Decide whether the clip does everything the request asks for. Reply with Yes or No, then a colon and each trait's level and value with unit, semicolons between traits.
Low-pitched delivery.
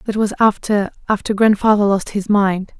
No: high, 205 Hz